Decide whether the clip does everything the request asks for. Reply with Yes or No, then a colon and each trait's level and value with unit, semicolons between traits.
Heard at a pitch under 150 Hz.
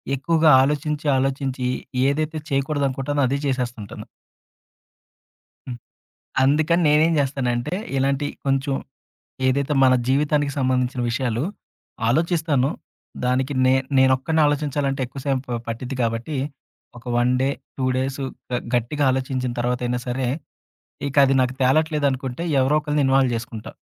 Yes: low, 135 Hz